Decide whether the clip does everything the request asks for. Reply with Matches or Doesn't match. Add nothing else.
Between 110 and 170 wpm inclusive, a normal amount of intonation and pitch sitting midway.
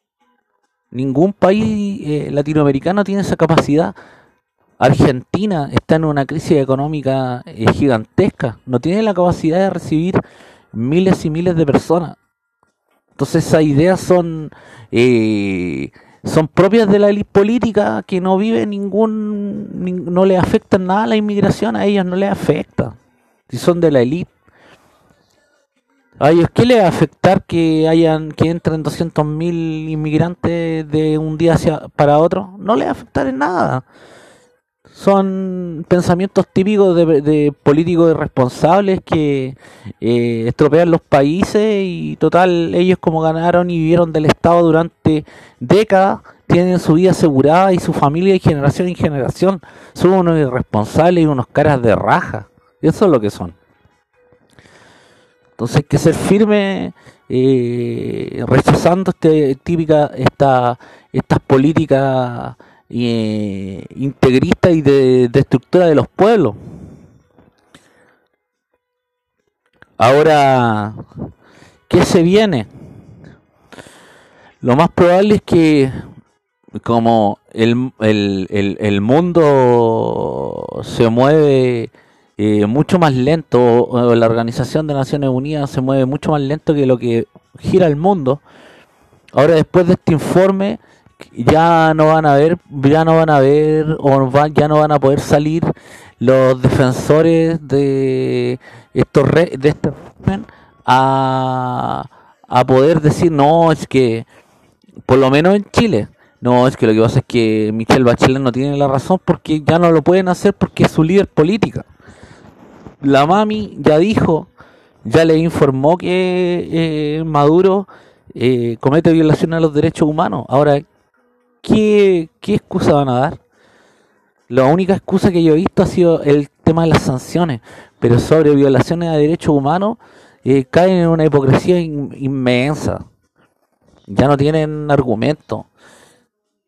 Matches